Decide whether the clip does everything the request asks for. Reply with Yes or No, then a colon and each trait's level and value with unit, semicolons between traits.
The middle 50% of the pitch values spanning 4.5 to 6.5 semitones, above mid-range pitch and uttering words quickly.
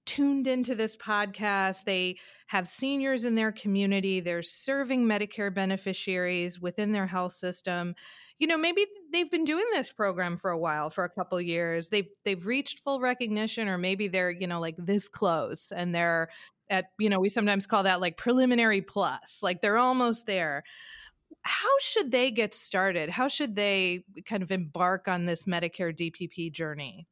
No: average, 5.1 semitones; high, 195 Hz; average, 175 wpm